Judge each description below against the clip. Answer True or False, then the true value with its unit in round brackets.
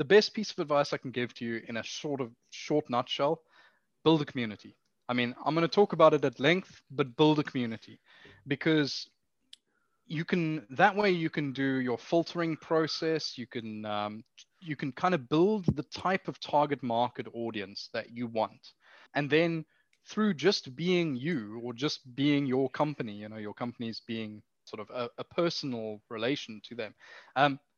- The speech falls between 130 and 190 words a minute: True (185 wpm)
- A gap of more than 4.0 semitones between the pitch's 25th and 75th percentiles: True (5.4 semitones)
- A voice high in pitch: False (140 Hz)